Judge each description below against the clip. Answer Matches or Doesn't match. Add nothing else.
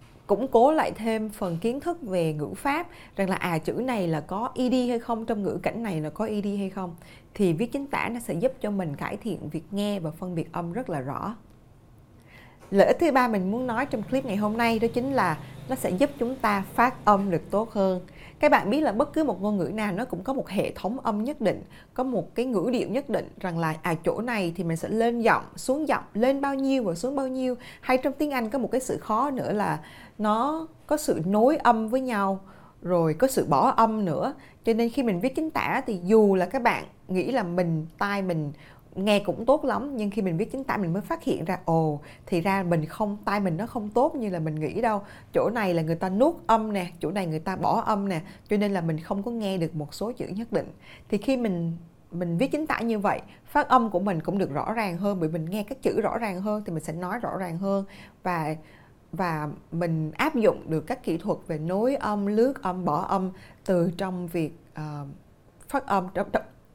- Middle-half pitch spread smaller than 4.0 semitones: Doesn't match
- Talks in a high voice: Matches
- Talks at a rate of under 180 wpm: Doesn't match